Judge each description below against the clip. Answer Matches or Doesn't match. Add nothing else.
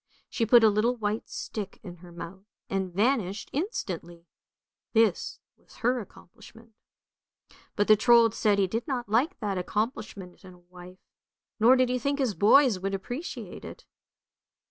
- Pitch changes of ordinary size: Matches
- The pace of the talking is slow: Doesn't match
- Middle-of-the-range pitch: Doesn't match